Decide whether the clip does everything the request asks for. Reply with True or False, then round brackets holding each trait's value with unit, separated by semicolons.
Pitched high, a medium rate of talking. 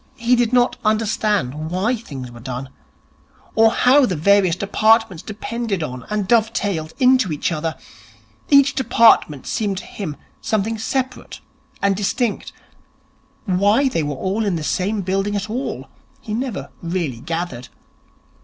True (205 Hz; 145 wpm)